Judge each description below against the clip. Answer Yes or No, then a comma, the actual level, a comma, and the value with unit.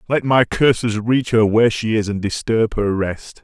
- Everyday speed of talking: No, fast, 210 wpm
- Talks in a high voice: No, low, 110 Hz